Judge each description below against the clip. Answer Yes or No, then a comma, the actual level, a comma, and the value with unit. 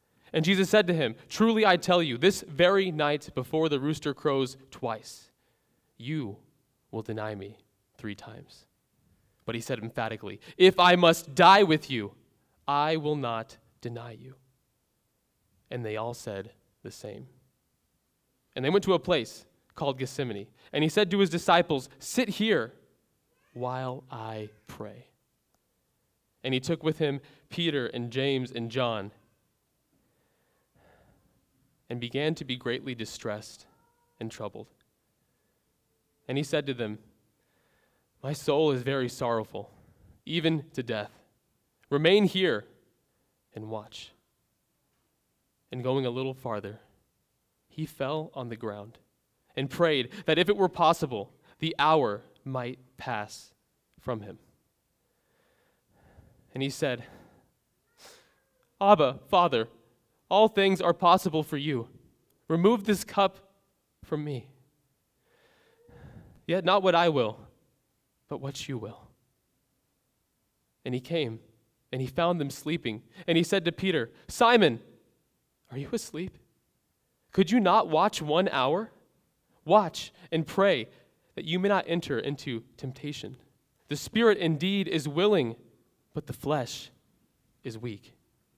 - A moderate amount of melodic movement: No, wide, 6.4 semitones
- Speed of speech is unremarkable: No, slow, 130 wpm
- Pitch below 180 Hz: Yes, medium, 140 Hz